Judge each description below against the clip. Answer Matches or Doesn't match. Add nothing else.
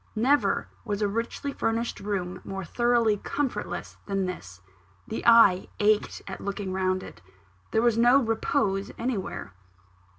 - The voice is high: Matches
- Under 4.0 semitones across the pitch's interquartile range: Matches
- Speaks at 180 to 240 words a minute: Doesn't match